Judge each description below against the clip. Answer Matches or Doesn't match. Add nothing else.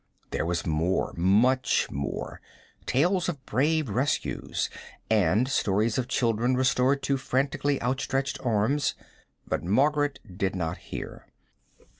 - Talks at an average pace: Doesn't match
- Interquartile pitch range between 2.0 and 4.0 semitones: Doesn't match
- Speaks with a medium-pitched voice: Doesn't match